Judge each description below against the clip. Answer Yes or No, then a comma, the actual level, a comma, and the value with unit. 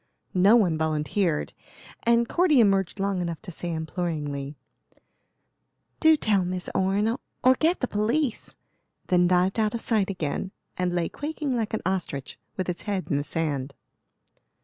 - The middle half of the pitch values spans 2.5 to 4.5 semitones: No, average, 5.1 semitones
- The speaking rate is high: No, average, 150 wpm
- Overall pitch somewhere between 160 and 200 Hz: Yes, high, 190 Hz